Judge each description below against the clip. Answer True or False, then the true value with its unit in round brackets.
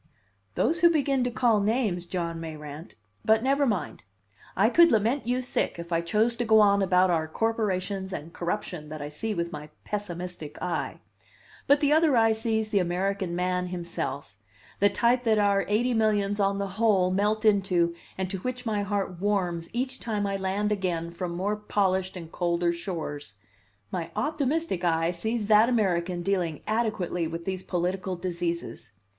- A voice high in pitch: True (195 Hz)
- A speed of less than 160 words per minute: False (170 wpm)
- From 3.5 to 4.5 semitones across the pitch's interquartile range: True (4.2 semitones)